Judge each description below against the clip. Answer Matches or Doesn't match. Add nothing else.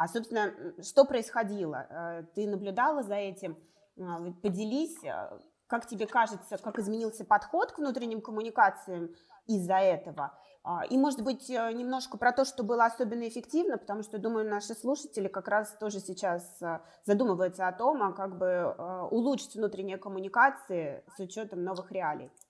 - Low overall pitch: Doesn't match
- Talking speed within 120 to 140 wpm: Matches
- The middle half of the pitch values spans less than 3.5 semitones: Doesn't match